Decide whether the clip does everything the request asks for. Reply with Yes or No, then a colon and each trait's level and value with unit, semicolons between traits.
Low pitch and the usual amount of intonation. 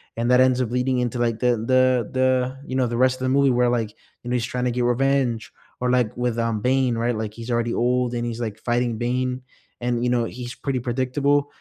No: low, 125 Hz; narrow, 1.5 semitones